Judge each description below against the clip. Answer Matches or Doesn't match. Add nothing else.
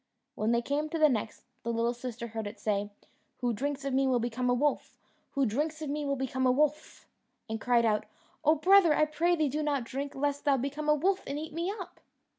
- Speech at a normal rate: Doesn't match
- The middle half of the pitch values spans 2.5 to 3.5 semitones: Doesn't match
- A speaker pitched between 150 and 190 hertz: Doesn't match